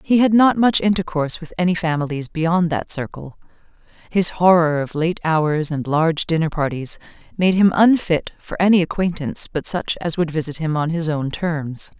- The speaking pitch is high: No, medium, 165 Hz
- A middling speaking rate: Yes, average, 180 wpm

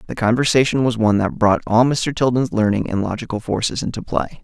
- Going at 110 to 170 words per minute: No, fast, 205 wpm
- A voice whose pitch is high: No, low, 115 Hz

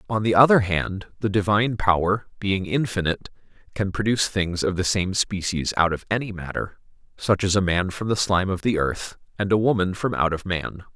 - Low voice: Yes, very low, 95 Hz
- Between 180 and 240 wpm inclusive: Yes, fast, 205 wpm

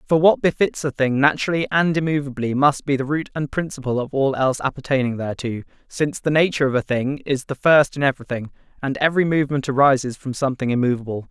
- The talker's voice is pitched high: No, medium, 140 Hz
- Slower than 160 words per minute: No, average, 195 wpm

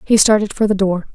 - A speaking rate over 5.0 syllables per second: Yes, 5.9 syllables/s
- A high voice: Yes, high, 200 Hz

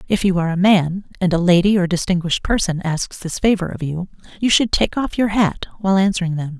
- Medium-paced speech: No, fast, 225 wpm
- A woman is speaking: Yes, female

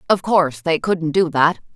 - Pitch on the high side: No, medium, 165 Hz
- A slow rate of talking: No, fast, 205 wpm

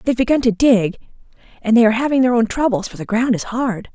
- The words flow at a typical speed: No, fast, 245 wpm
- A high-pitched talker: Yes, high, 230 Hz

